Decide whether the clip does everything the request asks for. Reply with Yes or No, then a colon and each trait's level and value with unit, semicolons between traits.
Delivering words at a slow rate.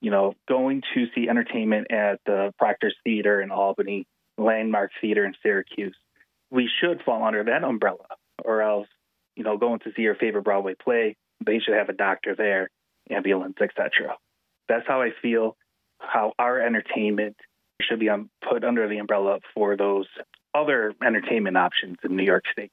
No: average, 165 wpm